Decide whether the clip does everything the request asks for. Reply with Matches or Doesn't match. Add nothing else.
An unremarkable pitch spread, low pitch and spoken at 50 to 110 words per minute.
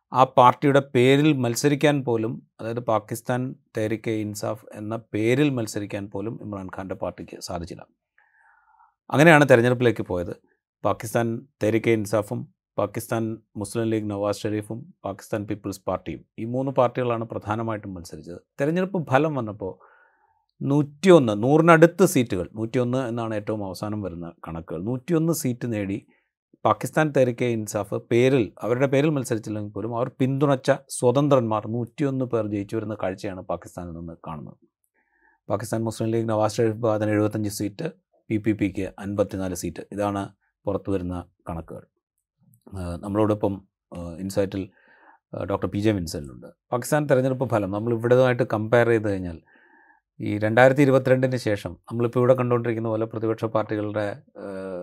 Doesn't match